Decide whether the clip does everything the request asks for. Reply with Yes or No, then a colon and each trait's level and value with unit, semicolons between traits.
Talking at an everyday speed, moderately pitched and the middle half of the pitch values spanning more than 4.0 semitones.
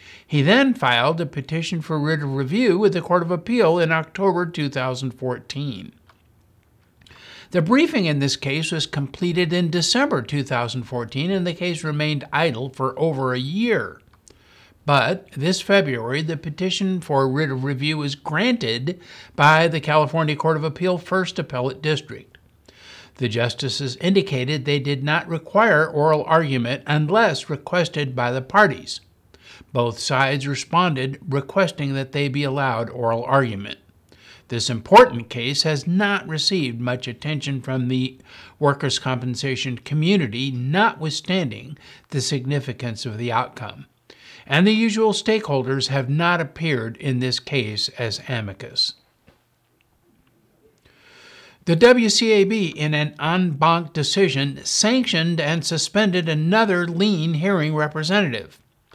No: slow, 125 wpm; medium, 150 Hz; average, 5.1 semitones